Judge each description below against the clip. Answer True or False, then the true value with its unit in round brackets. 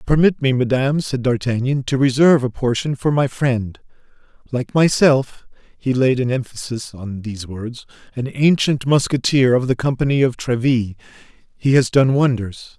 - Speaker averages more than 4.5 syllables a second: False (4.3 syllables/s)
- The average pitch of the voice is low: True (130 Hz)